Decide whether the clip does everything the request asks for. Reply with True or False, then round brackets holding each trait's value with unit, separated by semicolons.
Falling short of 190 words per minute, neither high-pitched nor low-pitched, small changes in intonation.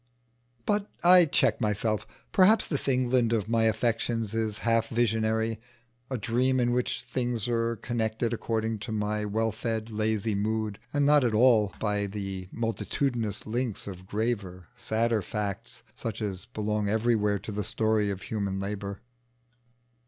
False (145 wpm; 110 Hz; 2.3 semitones)